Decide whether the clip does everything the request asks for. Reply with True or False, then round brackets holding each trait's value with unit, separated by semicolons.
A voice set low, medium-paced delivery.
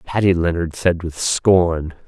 True (85 Hz; 145 wpm)